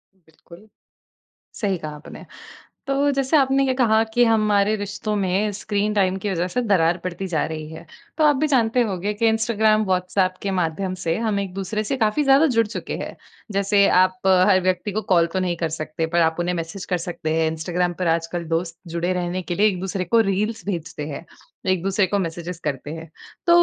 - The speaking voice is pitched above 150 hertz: Yes, high, 190 Hz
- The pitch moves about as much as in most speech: Yes, average, 3.8 semitones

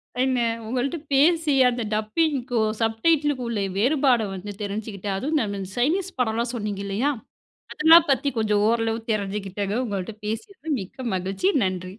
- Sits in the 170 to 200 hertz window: No, high, 230 Hz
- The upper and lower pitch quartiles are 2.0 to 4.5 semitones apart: No, average, 5.3 semitones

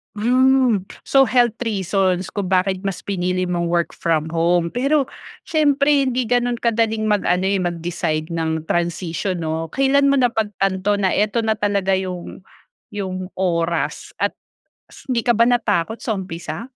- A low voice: No, high, 195 Hz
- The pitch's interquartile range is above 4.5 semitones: Yes, average, 5.2 semitones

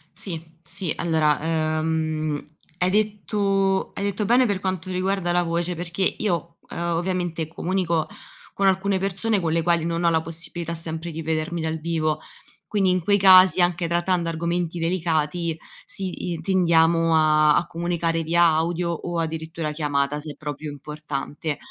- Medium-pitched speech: Yes, medium, 170 Hz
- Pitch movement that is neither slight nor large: No, narrow, 2.3 semitones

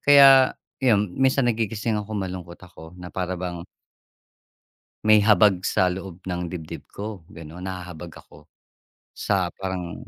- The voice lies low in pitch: Yes, very low, 95 Hz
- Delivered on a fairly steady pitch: No, average, 3.2 semitones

